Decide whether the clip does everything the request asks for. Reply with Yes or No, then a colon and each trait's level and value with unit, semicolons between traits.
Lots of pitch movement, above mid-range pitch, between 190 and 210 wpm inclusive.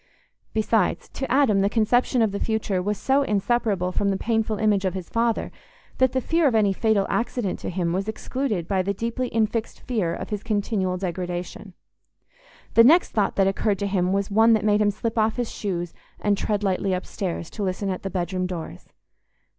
No: average, 3.1 semitones; high, 205 Hz; average, 195 wpm